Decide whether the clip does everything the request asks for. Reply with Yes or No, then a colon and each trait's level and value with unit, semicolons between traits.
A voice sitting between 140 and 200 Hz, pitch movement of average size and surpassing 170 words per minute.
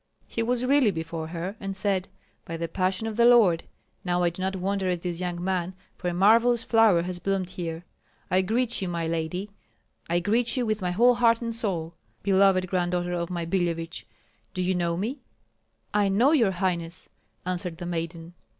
Yes: medium, 185 Hz; average, 3.4 semitones; average, 190 wpm